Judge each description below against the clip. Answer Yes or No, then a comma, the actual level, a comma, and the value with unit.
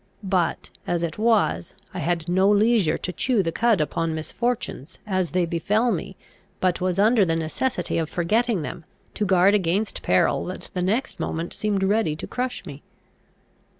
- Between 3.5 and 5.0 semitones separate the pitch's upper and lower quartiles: Yes, average, 4.3 semitones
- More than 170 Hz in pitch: Yes, medium, 185 Hz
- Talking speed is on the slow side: No, average, 170 wpm